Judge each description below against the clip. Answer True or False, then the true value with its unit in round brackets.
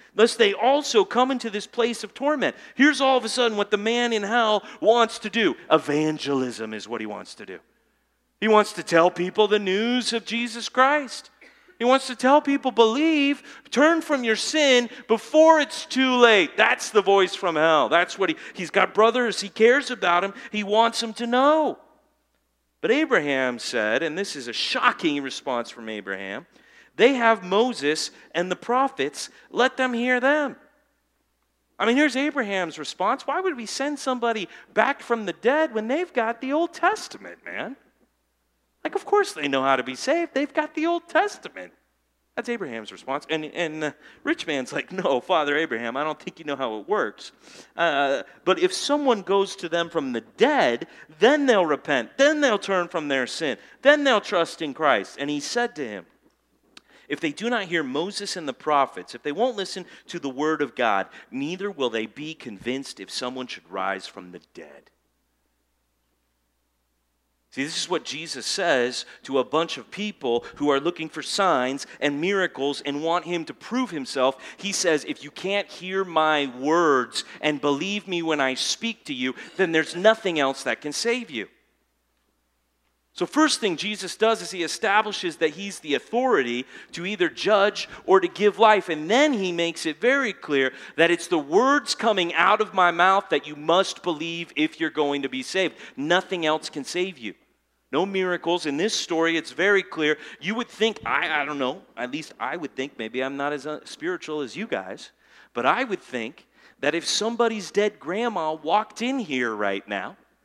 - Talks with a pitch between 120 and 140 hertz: False (195 Hz)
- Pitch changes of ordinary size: False (8.6 semitones)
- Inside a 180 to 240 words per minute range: True (190 wpm)